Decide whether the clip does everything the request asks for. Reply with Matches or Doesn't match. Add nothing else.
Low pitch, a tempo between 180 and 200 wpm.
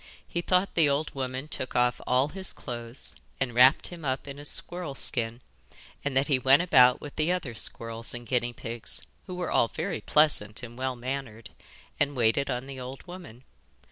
Matches